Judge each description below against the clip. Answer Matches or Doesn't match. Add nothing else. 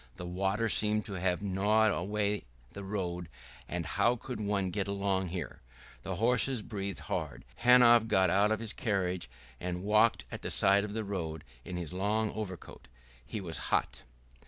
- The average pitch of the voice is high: Doesn't match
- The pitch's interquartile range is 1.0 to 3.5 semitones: Matches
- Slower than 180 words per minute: Matches